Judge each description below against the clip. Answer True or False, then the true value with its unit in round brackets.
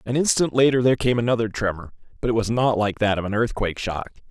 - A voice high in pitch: False (115 Hz)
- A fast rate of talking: True (235 wpm)